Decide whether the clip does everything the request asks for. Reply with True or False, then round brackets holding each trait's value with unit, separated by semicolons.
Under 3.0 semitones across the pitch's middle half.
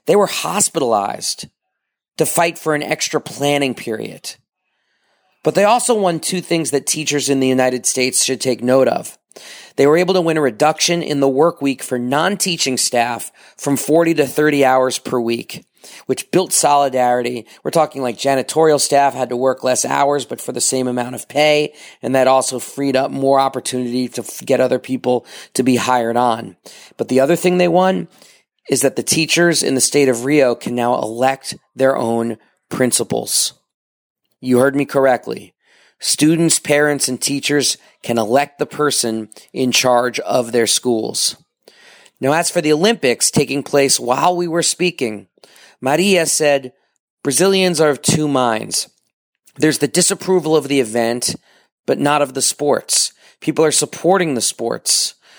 False (3.5 semitones)